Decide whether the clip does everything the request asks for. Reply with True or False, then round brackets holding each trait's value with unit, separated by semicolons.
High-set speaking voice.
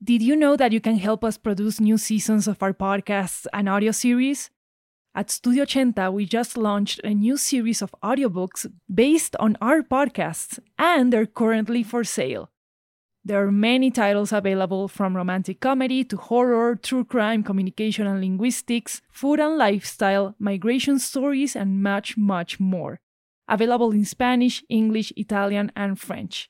True (220 Hz)